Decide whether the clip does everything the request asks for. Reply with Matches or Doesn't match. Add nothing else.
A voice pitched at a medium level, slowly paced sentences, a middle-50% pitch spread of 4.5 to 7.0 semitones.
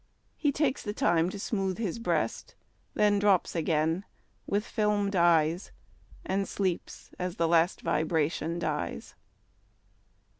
Doesn't match